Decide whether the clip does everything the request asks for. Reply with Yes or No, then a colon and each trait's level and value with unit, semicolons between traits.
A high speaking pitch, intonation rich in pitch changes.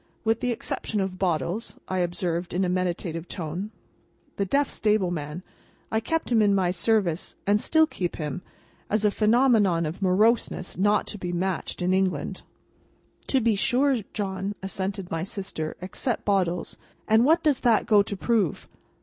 No: high, 195 Hz; average, 3.6 semitones